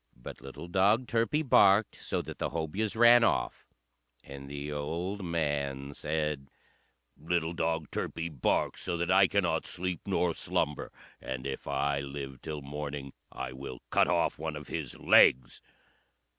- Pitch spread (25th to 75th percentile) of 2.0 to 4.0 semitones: No, average, 4.7 semitones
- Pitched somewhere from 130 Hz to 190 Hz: No, very low, 80 Hz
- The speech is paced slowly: No, average, 150 wpm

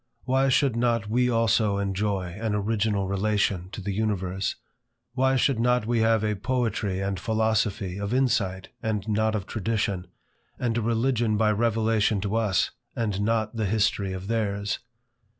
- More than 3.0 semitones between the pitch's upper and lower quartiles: No, narrow, 2.4 semitones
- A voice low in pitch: Yes, low, 110 Hz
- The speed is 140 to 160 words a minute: Yes, average, 155 wpm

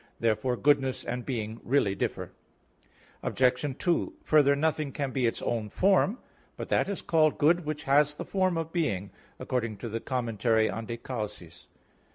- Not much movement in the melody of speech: No, average, 5.0 semitones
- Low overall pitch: Yes, low, 130 Hz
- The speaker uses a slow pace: No, average, 165 wpm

